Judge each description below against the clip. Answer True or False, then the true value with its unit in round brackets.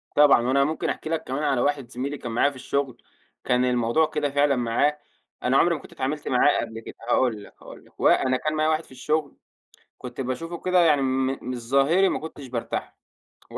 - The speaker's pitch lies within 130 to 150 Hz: True (140 Hz)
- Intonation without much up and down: False (3.2 semitones)